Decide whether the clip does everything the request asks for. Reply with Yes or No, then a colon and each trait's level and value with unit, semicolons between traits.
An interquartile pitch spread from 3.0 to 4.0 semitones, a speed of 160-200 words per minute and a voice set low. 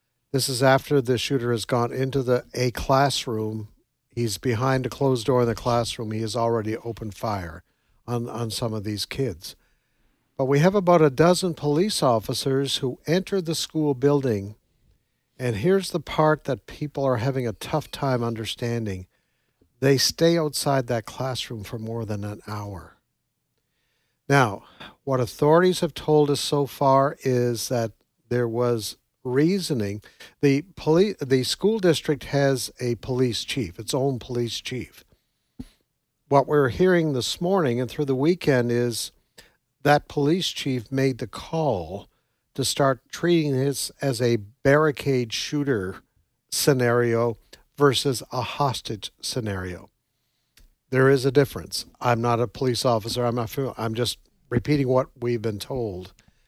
No: average, 3.5 semitones; average, 150 wpm; low, 130 Hz